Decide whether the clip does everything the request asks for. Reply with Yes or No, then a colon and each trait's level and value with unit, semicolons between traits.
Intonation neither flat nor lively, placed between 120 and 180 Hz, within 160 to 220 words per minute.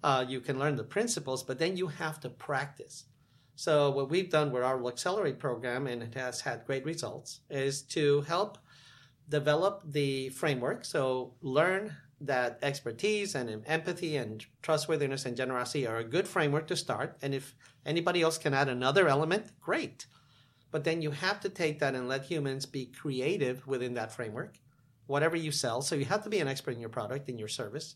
Yes: average, 3.6 semitones; medium, 140 Hz; average, 190 wpm